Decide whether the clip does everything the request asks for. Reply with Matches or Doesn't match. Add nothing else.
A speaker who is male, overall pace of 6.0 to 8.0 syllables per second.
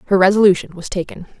Doesn't match